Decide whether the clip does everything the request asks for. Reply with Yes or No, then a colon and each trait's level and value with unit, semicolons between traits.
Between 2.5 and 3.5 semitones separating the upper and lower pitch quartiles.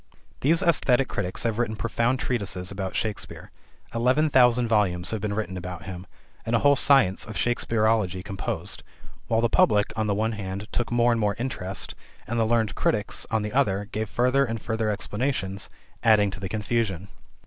Yes: average, 3.1 semitones